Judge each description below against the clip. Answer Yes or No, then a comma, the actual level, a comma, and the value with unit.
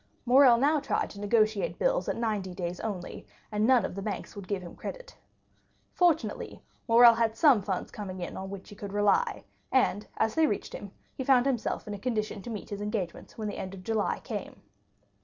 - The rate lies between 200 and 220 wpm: Yes, fast, 205 wpm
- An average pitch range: Yes, average, 3.7 semitones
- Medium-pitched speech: No, high, 215 Hz